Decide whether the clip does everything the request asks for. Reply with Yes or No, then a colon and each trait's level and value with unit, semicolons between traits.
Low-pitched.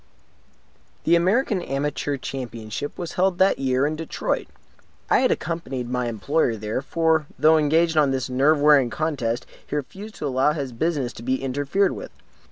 No: medium, 145 Hz